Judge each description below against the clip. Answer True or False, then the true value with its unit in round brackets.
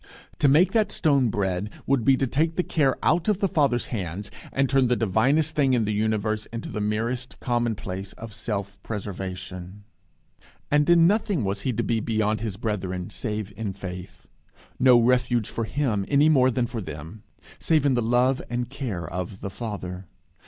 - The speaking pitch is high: False (115 Hz)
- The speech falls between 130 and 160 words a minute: False (180 wpm)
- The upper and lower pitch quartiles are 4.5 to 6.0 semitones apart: True (5.0 semitones)